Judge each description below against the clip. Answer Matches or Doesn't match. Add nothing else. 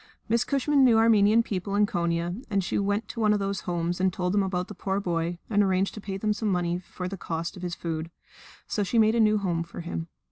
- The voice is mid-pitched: Doesn't match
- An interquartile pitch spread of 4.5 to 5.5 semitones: Doesn't match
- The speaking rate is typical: Doesn't match